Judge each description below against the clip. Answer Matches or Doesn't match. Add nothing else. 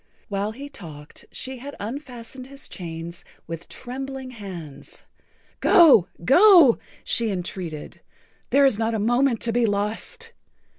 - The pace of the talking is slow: Matches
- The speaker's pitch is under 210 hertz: Doesn't match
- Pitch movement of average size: Doesn't match